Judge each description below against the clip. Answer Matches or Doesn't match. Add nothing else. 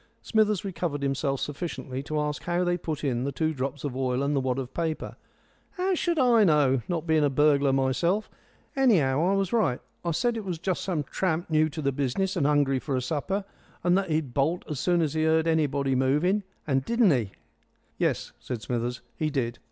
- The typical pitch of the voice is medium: Matches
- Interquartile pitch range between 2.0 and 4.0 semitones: Doesn't match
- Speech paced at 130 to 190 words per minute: Doesn't match